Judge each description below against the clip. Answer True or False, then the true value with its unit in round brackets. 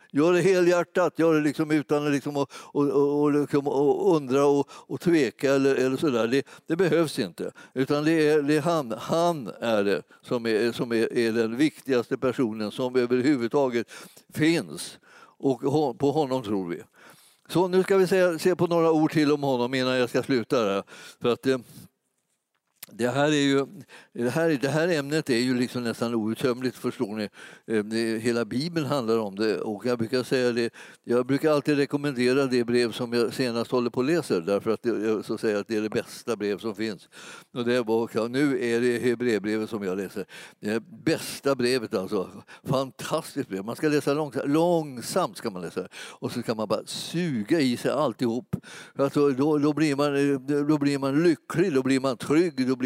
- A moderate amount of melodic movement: True (4.0 semitones)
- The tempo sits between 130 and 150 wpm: False (190 wpm)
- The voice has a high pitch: False (135 Hz)